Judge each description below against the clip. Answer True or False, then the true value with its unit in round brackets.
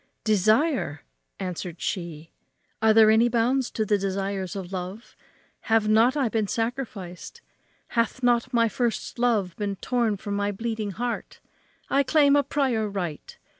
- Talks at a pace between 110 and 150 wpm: True (145 wpm)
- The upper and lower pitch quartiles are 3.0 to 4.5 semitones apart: True (3.8 semitones)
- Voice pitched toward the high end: True (220 Hz)